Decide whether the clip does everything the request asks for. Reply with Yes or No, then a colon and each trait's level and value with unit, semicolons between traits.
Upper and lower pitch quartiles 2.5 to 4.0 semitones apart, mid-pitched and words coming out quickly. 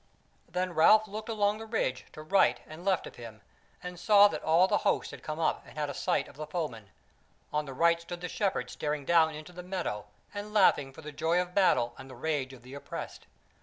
No: average, 4.8 semitones; medium, 165 Hz; fast, 230 wpm